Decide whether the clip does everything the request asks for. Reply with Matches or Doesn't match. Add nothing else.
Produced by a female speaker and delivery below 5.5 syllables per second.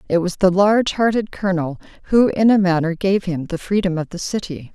Doesn't match